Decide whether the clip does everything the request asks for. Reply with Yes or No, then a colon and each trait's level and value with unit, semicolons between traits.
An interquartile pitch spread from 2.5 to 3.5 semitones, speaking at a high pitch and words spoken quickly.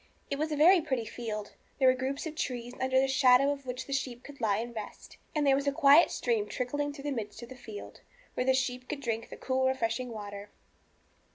Yes: average, 3.0 semitones; very high, 260 Hz; fast, 235 wpm